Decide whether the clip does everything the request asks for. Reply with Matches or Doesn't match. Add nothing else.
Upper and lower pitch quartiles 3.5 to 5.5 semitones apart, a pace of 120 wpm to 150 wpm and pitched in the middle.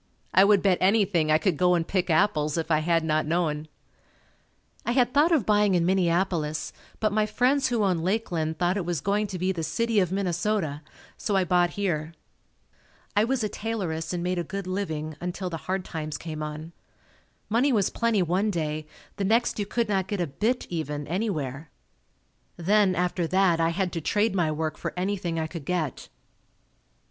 Doesn't match